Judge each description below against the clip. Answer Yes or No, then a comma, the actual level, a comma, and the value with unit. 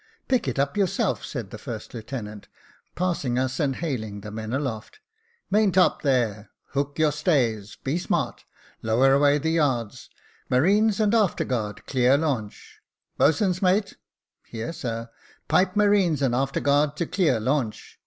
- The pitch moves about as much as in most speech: No, wide, 7.0 semitones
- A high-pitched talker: No, medium, 140 Hz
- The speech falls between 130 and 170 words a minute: Yes, average, 160 wpm